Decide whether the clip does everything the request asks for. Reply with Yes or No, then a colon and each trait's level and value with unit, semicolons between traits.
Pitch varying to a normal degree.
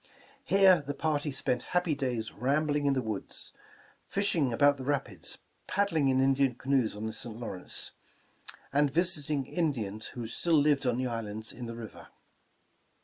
Yes: average, 4.0 semitones